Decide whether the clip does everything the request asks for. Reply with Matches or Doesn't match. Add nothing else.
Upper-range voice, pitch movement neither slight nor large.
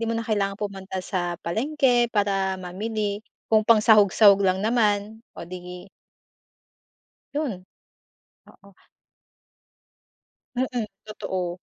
Matches